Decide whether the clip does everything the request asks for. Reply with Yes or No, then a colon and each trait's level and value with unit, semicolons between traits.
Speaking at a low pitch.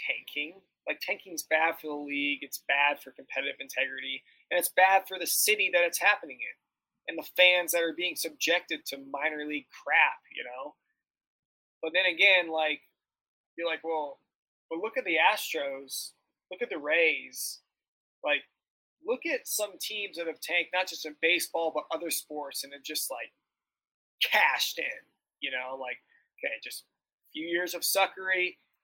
No: medium, 165 Hz